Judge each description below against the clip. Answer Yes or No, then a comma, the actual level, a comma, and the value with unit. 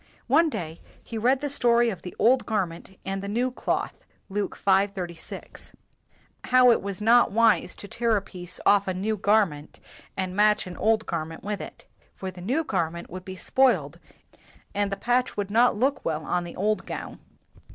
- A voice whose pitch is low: No, high, 205 Hz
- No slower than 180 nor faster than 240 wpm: Yes, average, 195 wpm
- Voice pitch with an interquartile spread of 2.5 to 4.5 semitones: Yes, average, 4.2 semitones